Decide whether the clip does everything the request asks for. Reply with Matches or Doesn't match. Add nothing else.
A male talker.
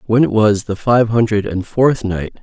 Matches